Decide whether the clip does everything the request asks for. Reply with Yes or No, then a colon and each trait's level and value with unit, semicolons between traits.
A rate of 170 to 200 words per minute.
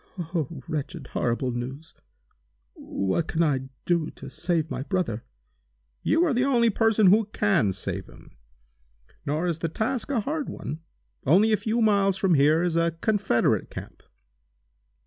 No: average, 150 wpm